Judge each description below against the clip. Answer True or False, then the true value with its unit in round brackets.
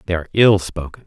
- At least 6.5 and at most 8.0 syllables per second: True (7.1 syllables/s)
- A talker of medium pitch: False (90 Hz)